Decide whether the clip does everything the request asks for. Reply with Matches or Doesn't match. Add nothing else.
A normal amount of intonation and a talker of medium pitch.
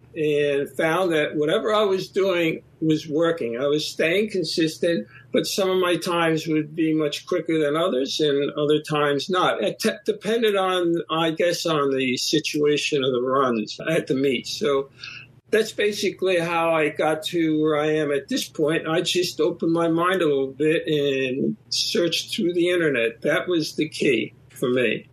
Matches